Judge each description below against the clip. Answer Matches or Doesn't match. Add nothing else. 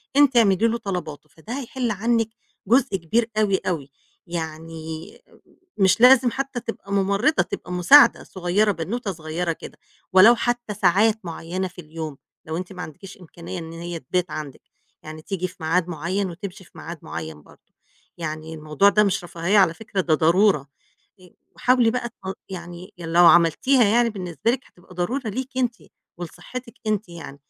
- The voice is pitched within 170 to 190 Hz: Matches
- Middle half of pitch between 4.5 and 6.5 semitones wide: Matches